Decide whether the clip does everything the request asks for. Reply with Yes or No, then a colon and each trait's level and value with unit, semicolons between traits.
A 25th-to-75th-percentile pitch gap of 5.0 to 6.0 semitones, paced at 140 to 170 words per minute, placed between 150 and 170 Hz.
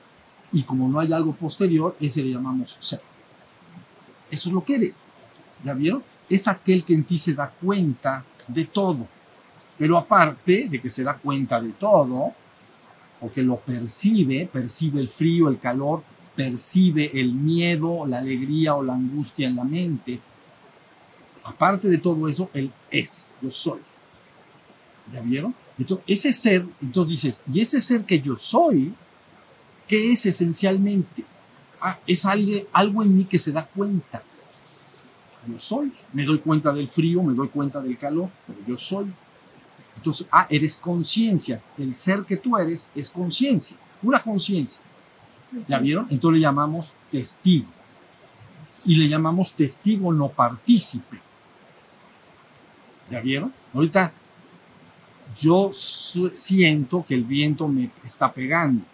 Yes: wide, 5.5 semitones; average, 145 wpm; medium, 160 Hz